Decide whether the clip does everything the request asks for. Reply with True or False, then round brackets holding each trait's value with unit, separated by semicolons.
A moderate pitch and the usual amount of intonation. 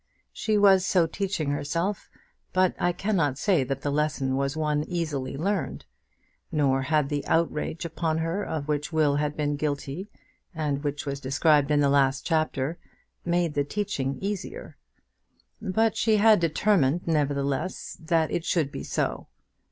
True (155 Hz; 3.7 semitones)